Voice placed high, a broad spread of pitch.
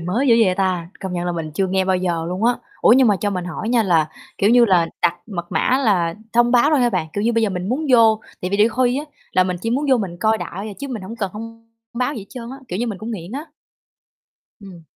No: high, 210 Hz; average, 4.6 semitones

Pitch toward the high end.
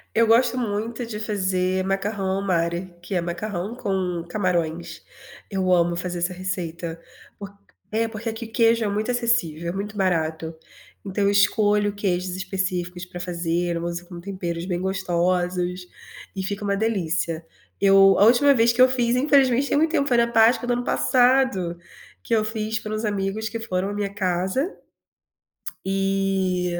Yes: high, 195 Hz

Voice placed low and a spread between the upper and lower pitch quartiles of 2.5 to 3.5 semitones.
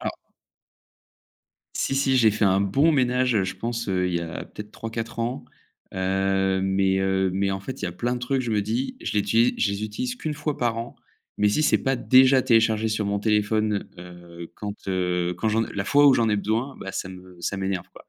No: low, 105 Hz; average, 4.1 semitones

